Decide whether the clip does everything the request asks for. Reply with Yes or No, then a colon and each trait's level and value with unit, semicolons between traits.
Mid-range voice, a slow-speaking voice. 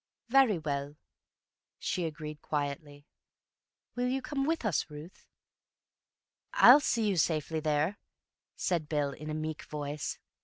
Yes: medium, 155 Hz; slow, 125 wpm